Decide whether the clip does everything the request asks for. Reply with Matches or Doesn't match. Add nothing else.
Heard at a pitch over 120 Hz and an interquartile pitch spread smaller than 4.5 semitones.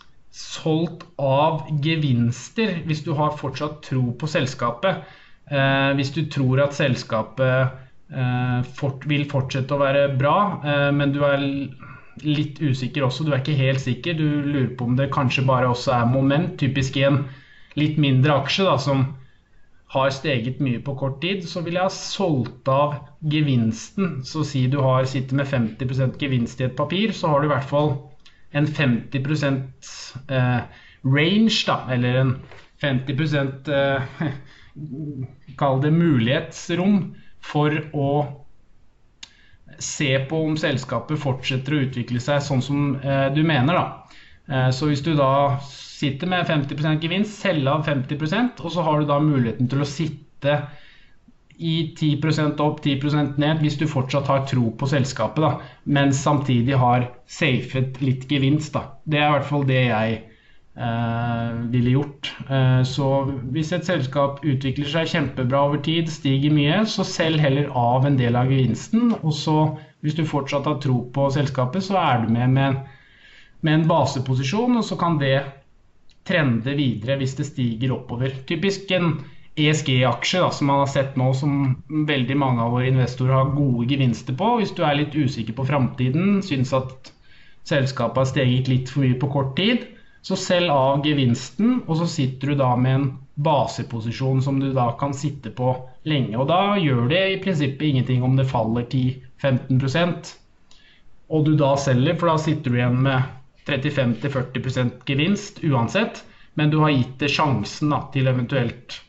Matches